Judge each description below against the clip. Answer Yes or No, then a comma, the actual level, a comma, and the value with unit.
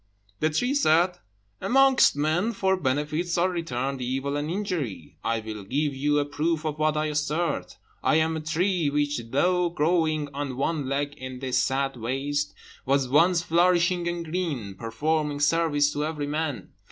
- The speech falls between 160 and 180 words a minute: Yes, average, 165 wpm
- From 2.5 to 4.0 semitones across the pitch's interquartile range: Yes, average, 3.5 semitones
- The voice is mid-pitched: Yes, medium, 150 Hz